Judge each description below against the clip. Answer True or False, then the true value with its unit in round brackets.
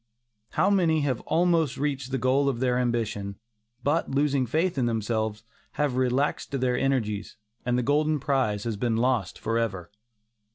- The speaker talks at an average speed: True (155 wpm)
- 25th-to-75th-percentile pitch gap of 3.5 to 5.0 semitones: True (3.8 semitones)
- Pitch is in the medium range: False (130 Hz)